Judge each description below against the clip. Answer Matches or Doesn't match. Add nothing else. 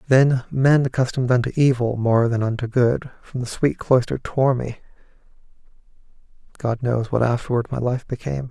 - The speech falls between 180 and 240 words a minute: Doesn't match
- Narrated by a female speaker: Doesn't match